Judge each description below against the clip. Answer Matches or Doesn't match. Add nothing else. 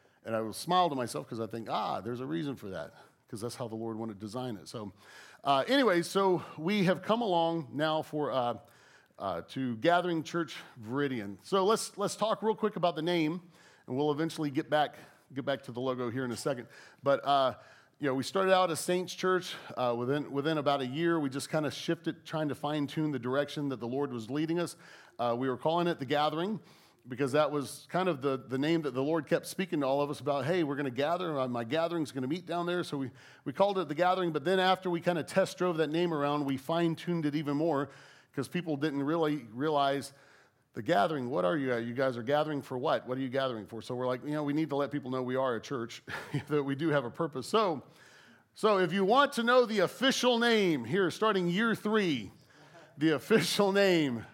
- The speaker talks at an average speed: Doesn't match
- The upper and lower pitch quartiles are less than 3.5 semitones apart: Doesn't match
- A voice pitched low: Doesn't match